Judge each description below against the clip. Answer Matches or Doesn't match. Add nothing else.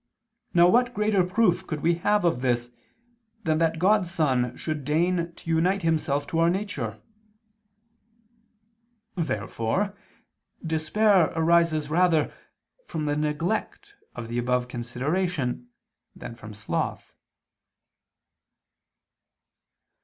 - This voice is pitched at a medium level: Matches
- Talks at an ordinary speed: Doesn't match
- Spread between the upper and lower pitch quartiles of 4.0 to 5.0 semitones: Doesn't match